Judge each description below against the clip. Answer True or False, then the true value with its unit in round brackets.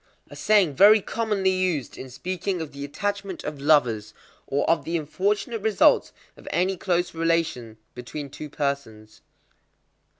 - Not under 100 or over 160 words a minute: True (140 wpm)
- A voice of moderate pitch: True (165 Hz)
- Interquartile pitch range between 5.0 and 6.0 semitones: True (5.4 semitones)